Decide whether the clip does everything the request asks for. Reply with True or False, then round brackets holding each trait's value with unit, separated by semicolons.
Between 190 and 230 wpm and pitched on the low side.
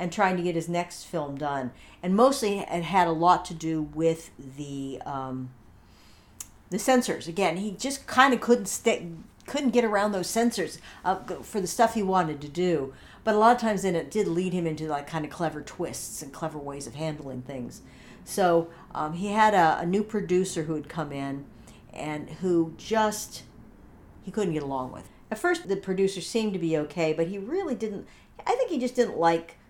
False (205 wpm; 175 Hz)